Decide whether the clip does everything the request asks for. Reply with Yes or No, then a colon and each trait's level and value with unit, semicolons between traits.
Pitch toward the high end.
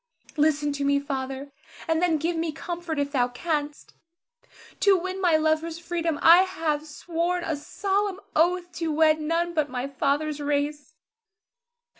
Yes: very high, 315 Hz